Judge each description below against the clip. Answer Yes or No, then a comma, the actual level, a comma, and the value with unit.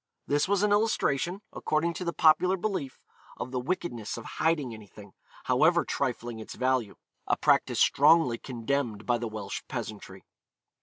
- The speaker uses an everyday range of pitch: No, wide, 6.7 semitones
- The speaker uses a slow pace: No, average, 150 wpm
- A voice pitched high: No, low, 130 Hz